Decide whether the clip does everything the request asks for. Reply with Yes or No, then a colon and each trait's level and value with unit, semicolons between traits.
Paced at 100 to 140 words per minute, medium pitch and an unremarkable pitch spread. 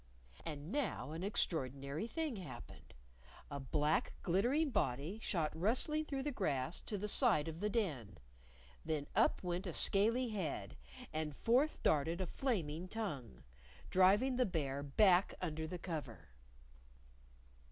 No: slow, 135 wpm; medium, 175 Hz; wide, 6.9 semitones